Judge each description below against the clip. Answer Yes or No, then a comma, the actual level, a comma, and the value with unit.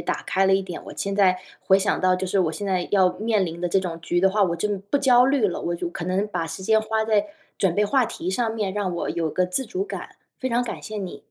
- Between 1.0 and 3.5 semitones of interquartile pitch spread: Yes, average, 3.1 semitones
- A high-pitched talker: Yes, high, 195 Hz